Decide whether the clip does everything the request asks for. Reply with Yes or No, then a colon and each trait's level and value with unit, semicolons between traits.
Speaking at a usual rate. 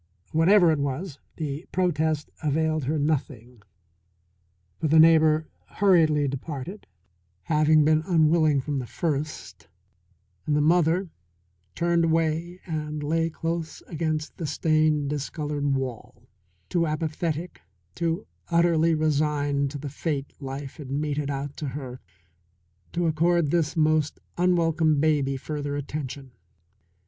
No: slow, 120 wpm